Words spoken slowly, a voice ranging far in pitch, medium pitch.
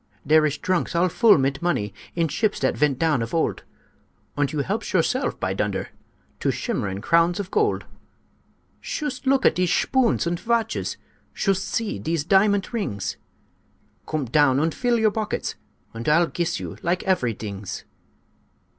No: average, 160 wpm; wide, 6.5 semitones; medium, 170 Hz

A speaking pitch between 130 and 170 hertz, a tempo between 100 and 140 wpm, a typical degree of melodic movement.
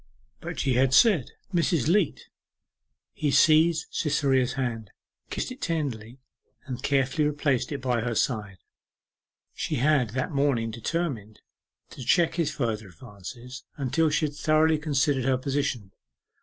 Yes: low, 135 Hz; slow, 135 wpm; average, 4.1 semitones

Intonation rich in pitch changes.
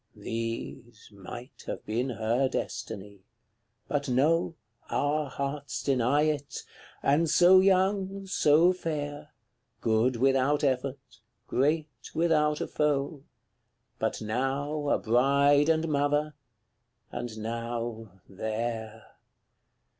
No: average, 4.4 semitones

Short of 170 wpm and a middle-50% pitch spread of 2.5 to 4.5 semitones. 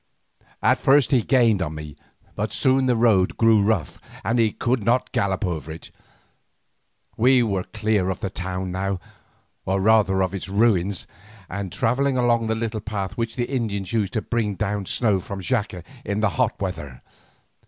No: average, 175 wpm; average, 3.5 semitones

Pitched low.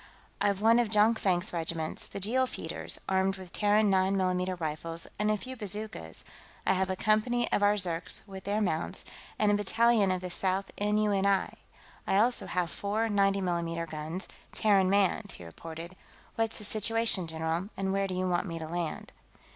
No: high, 195 Hz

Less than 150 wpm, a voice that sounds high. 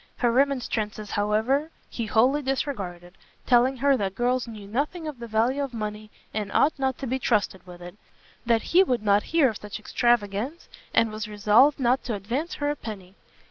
No: average, 185 wpm; high, 235 Hz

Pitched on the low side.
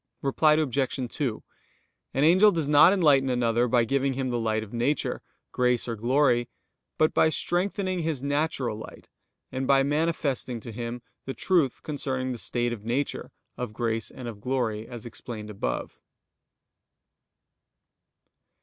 Yes: low, 130 Hz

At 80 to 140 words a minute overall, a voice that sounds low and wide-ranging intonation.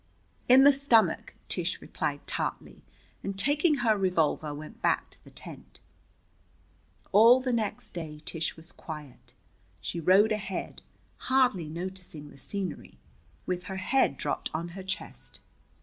No: slow, 135 wpm; high, 190 Hz; wide, 6.2 semitones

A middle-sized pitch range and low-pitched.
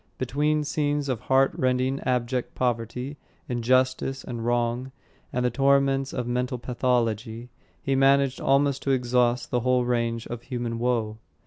No: narrow, 2.1 semitones; low, 125 Hz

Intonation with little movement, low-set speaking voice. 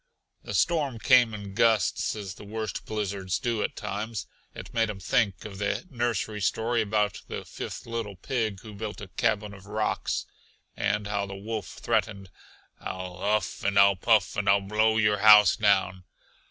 Yes: narrow, 2.0 semitones; low, 105 Hz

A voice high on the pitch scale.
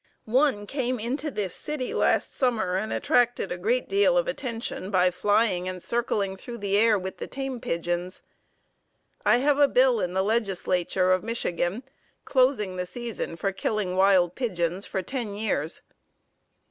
Yes: high, 210 Hz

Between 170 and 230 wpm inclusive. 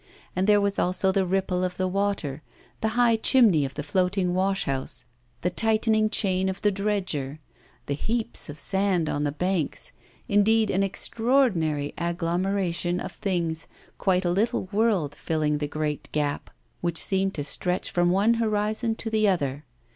No: average, 160 wpm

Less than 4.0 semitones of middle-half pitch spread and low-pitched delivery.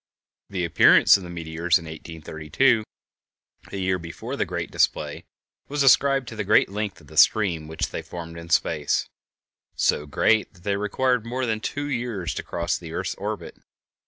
No: average, 5.2 semitones; very low, 95 Hz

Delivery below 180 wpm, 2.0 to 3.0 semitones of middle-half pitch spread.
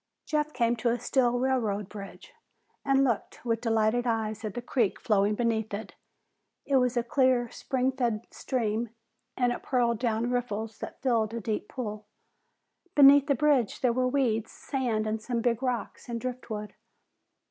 Yes: average, 160 wpm; narrow, 2.6 semitones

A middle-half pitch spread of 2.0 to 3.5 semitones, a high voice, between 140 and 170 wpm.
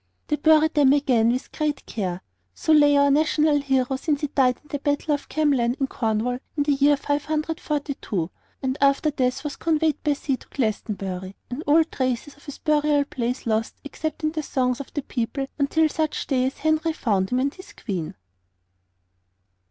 No: average, 3.2 semitones; very high, 280 Hz; average, 185 wpm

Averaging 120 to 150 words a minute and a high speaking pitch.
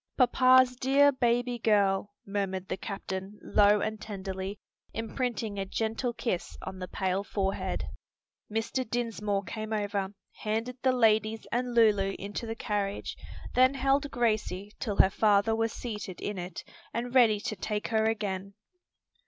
Yes: average, 145 wpm; high, 215 Hz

